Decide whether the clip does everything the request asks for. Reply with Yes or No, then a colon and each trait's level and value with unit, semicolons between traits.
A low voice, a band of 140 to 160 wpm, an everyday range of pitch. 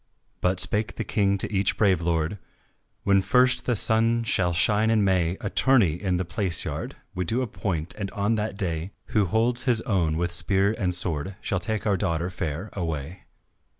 No: very low, 95 Hz; average, 185 wpm; average, 3.8 semitones